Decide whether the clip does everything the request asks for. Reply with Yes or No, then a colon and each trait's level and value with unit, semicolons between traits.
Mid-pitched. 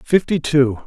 Yes: medium, 145 Hz